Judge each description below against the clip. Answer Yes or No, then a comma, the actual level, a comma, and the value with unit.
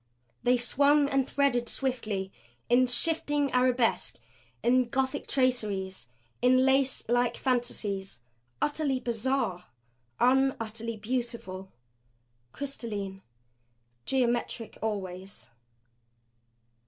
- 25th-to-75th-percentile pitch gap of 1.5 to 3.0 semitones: No, average, 3.7 semitones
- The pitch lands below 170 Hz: No, high, 245 Hz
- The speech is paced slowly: Yes, slow, 80 wpm